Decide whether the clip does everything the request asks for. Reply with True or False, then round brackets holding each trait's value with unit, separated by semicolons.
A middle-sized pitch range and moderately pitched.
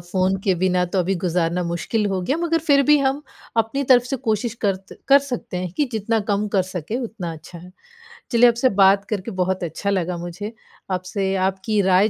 False (4.0 semitones; 195 Hz)